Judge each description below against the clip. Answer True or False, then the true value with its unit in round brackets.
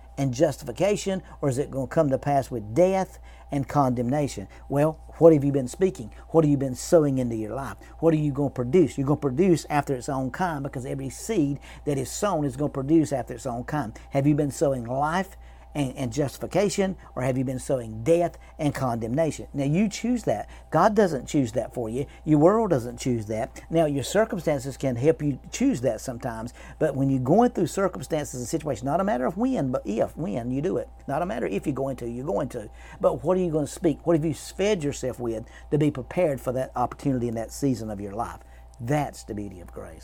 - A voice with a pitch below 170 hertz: True (140 Hz)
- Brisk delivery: True (230 wpm)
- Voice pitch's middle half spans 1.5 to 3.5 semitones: False (4.3 semitones)